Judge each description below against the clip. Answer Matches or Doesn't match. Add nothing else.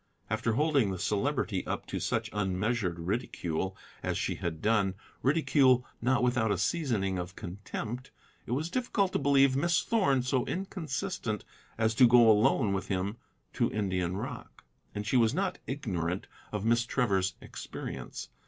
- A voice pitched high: Doesn't match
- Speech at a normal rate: Matches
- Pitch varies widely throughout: Matches